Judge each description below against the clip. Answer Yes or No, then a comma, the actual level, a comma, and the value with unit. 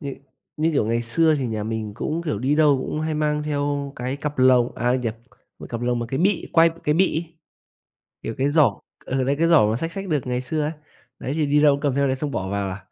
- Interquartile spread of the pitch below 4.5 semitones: Yes, average, 4.0 semitones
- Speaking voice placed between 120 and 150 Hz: Yes, medium, 140 Hz